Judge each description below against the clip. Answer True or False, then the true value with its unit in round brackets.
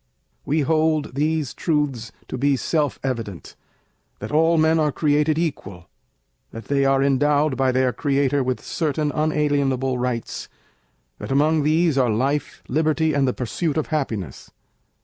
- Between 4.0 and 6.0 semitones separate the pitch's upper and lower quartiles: False (3.0 semitones)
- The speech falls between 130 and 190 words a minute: True (145 wpm)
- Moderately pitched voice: True (145 Hz)